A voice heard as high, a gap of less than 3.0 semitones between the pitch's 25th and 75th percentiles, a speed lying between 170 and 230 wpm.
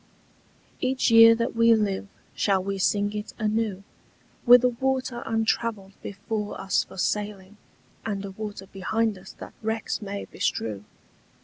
No: high, 210 Hz; narrow, 2.6 semitones; average, 140 wpm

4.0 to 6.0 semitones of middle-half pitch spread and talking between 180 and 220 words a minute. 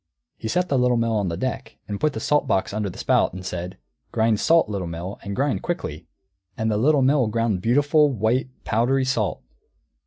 Yes: average, 5.1 semitones; average, 190 wpm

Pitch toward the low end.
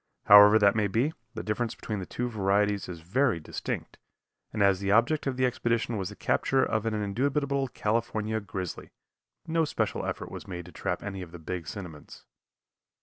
Yes: low, 105 Hz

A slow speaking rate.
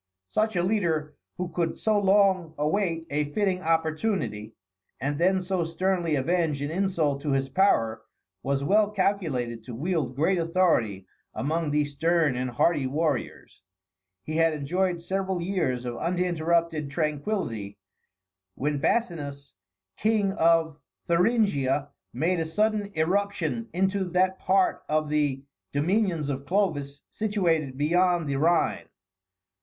Yes: slow, 130 wpm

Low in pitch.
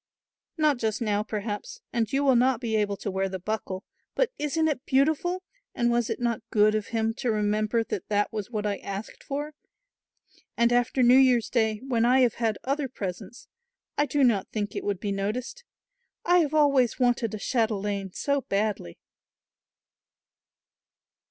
No: high, 230 Hz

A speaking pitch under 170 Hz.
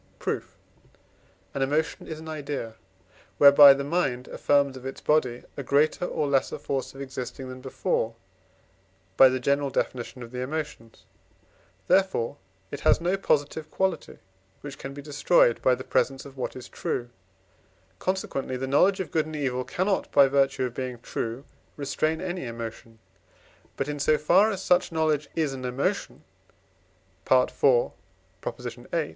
Yes: medium, 140 Hz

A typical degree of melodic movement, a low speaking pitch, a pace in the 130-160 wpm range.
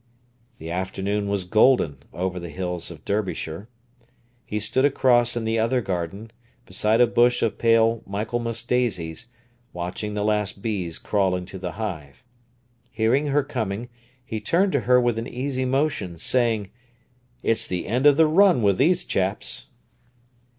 Yes: average, 4.6 semitones; low, 110 Hz; average, 150 wpm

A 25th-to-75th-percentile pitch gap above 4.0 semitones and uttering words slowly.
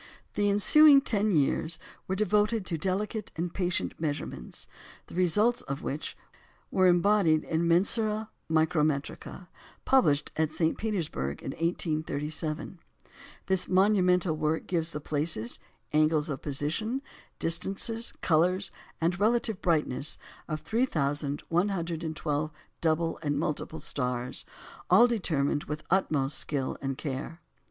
Yes: average, 4.4 semitones; slow, 115 wpm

